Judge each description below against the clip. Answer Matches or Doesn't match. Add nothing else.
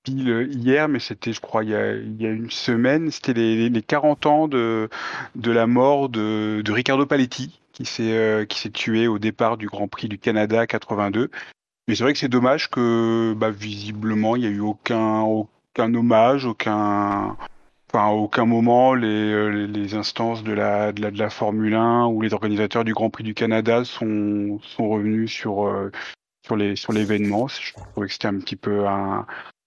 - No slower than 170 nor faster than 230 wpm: Matches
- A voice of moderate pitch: Doesn't match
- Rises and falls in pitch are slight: Matches